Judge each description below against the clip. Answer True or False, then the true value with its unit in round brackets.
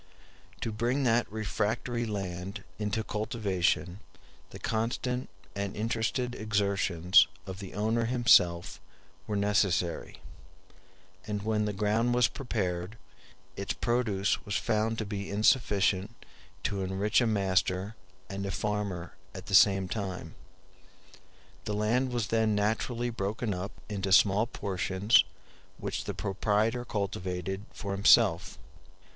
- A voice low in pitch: True (105 Hz)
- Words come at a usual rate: False (120 wpm)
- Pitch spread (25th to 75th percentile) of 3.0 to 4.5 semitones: False (2.6 semitones)